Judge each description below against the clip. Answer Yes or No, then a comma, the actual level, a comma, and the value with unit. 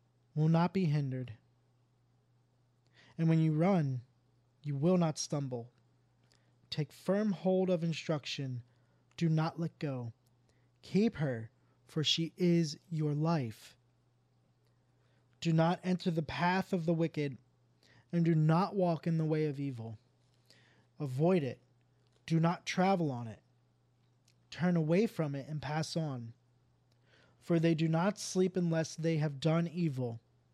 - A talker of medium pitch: Yes, medium, 145 Hz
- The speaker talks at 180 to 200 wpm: No, slow, 135 wpm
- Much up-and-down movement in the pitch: No, average, 5.0 semitones